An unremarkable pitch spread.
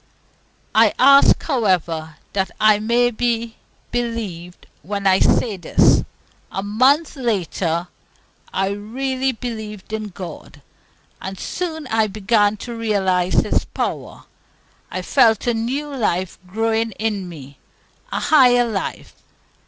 Yes: average, 4.1 semitones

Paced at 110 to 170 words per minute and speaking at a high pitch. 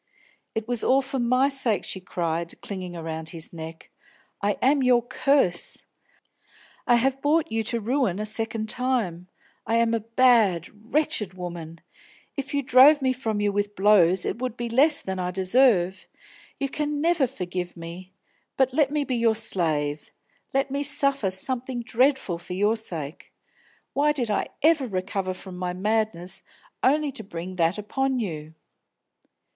Yes: average, 160 wpm; high, 220 Hz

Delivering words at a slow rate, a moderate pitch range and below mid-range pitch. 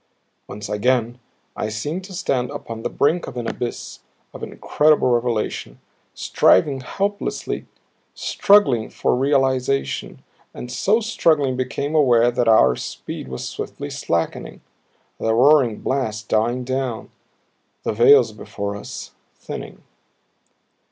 Yes: slow, 120 wpm; average, 4.0 semitones; low, 125 Hz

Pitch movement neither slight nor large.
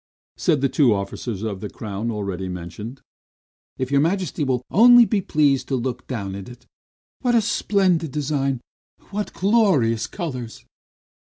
No: wide, 7.5 semitones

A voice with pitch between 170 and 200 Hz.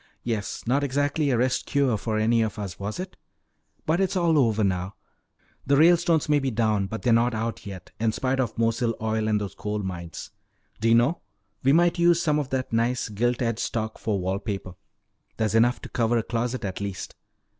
No: low, 115 Hz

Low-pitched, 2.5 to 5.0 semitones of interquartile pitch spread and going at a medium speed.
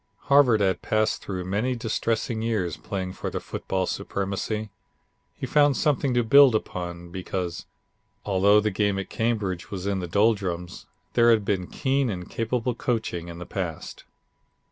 Yes: low, 100 Hz; average, 3.8 semitones; average, 155 wpm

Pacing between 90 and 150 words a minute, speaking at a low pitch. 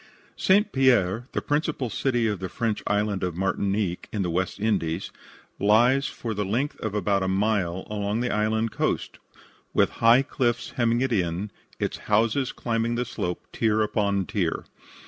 No: average, 165 wpm; low, 110 Hz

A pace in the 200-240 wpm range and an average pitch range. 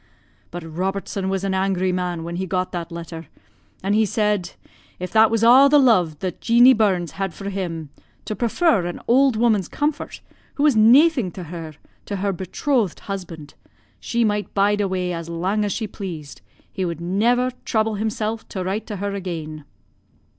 No: average, 175 wpm; average, 3.9 semitones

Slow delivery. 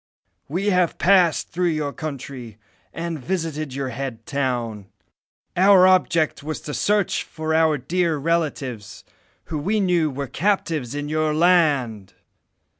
Yes: slow, 130 wpm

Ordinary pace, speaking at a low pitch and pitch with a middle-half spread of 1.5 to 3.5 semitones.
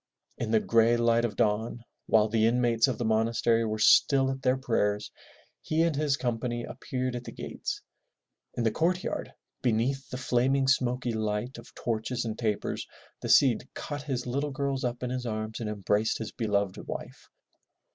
Yes: average, 175 wpm; low, 120 Hz; average, 2.8 semitones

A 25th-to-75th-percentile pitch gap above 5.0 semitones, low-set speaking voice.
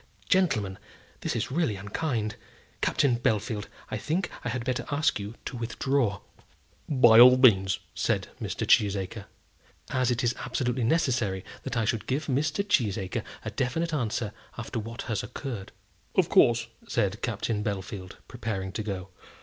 No: average, 3.9 semitones; low, 115 Hz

